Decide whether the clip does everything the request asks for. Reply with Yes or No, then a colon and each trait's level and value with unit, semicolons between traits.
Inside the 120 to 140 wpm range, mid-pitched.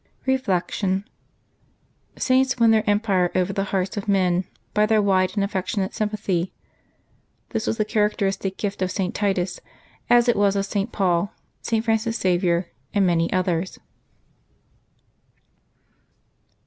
No: slow, 135 wpm; high, 200 Hz